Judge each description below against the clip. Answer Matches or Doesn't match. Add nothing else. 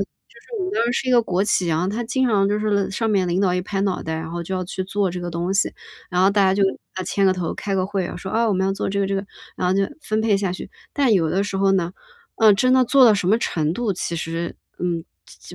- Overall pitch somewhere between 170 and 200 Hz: Matches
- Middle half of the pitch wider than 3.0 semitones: Doesn't match